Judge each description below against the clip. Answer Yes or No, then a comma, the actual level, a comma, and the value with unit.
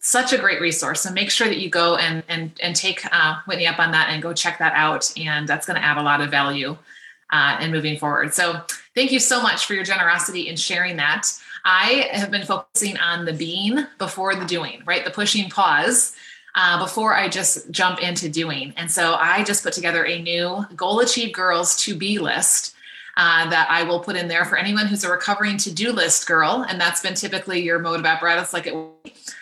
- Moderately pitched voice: Yes, medium, 175 Hz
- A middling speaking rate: No, fast, 225 wpm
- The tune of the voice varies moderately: Yes, average, 3.2 semitones